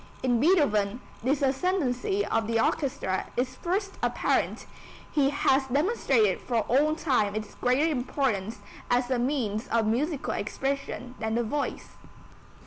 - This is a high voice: Yes, very high, 255 Hz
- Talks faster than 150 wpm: No, slow, 135 wpm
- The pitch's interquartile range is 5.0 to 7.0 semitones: No, average, 4.2 semitones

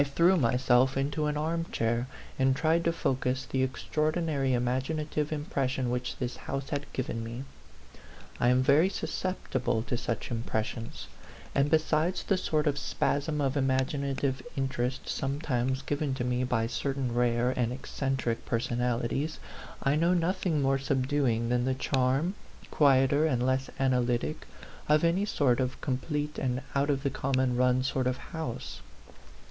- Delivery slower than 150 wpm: No, average, 155 wpm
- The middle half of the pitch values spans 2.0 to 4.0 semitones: Yes, average, 3.0 semitones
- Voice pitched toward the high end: No, low, 135 Hz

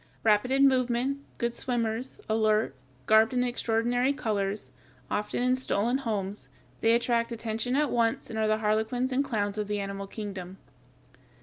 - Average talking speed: Yes, average, 150 wpm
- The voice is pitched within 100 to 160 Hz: No, high, 225 Hz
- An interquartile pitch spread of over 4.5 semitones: No, average, 2.9 semitones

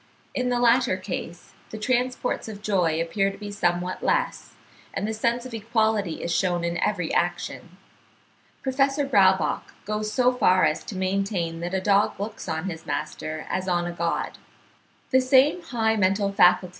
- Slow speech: No, average, 165 wpm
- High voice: Yes, high, 200 Hz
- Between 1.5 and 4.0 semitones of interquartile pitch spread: No, average, 4.4 semitones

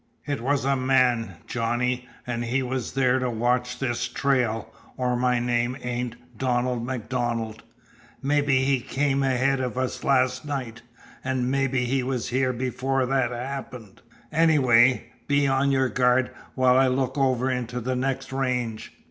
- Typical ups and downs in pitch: No, narrow, 1.6 semitones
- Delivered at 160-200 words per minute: No, average, 150 wpm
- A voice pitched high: No, low, 125 Hz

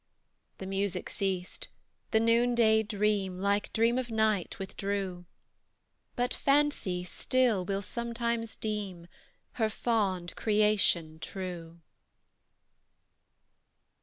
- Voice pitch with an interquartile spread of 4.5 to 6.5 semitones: No, average, 3.5 semitones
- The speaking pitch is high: Yes, high, 205 Hz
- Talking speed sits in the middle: No, slow, 90 wpm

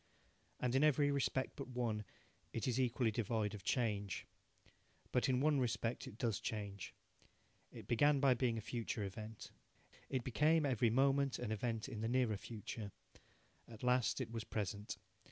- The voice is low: Yes, low, 120 Hz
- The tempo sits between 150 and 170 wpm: Yes, average, 160 wpm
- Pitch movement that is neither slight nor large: Yes, average, 3.3 semitones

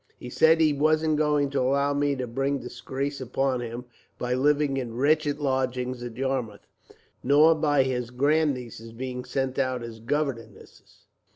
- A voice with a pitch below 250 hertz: Yes, low, 135 Hz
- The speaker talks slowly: No, average, 155 wpm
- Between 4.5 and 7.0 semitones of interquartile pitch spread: No, average, 2.7 semitones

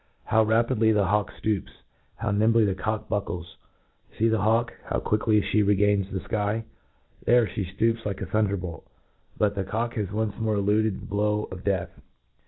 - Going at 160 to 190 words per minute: Yes, average, 175 wpm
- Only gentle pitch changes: Yes, narrow, 2.0 semitones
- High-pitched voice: No, low, 105 Hz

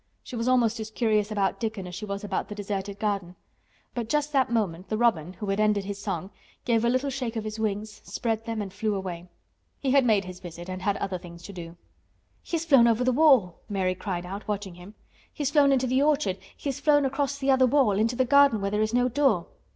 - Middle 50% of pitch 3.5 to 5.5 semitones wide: Yes, average, 4.5 semitones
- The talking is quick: Yes, fast, 235 wpm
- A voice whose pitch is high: Yes, high, 215 Hz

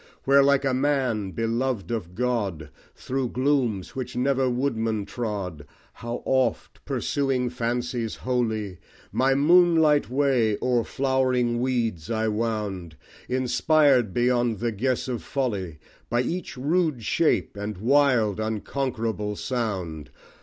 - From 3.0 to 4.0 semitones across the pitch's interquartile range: Yes, average, 3.6 semitones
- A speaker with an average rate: No, slow, 120 wpm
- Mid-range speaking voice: No, low, 120 Hz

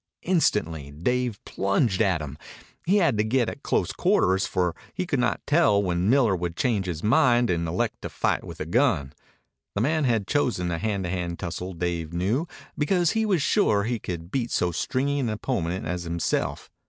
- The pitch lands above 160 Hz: No, low, 100 Hz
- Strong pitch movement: Yes, wide, 6.7 semitones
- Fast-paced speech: No, average, 190 wpm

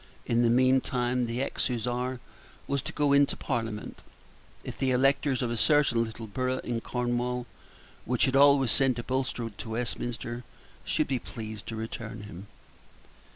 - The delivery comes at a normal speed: Yes, average, 155 wpm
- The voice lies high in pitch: No, low, 125 Hz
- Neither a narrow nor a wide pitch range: No, narrow, 2.1 semitones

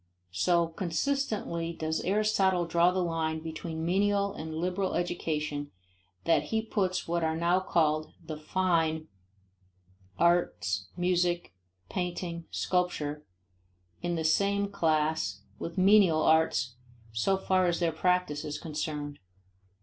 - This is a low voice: No, medium, 170 Hz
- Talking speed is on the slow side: Yes, slow, 120 wpm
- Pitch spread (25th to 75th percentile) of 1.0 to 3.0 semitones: Yes, average, 2.7 semitones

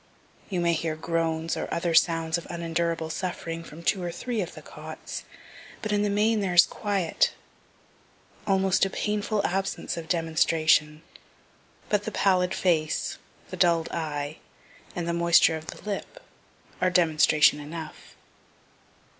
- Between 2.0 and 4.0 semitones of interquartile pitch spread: Yes, average, 2.9 semitones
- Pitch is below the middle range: No, medium, 170 Hz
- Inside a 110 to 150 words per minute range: Yes, average, 145 wpm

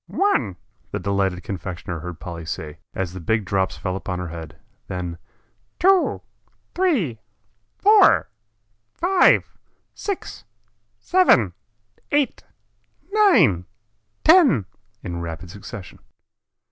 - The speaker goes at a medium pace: No, slow, 100 wpm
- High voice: No, very low, 95 Hz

